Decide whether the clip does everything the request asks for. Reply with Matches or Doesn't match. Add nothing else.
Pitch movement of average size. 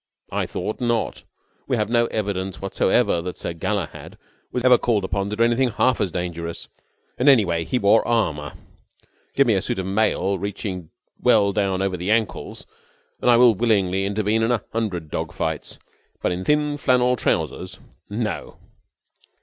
Matches